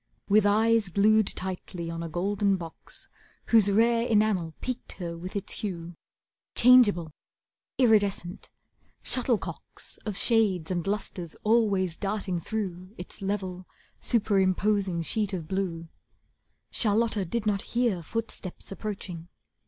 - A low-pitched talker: No, high, 200 Hz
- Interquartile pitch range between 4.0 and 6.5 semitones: No, average, 3.3 semitones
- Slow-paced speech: Yes, slow, 115 wpm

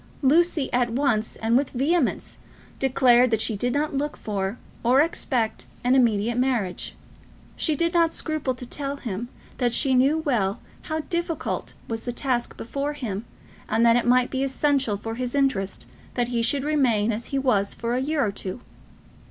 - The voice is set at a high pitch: Yes, very high, 250 Hz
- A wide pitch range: No, average, 3.6 semitones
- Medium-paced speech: Yes, average, 175 wpm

